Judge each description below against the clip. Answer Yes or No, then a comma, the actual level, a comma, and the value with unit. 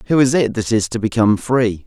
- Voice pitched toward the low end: Yes, low, 115 Hz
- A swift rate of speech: Yes, fast, 255 wpm